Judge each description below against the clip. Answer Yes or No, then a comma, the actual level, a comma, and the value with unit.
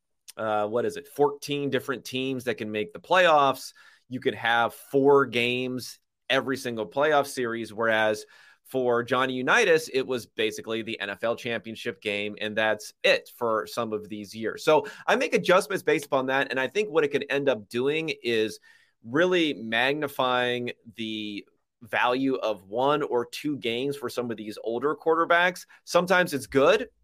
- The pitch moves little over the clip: No, average, 4.2 semitones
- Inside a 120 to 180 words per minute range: Yes, average, 165 wpm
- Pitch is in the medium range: No, low, 125 Hz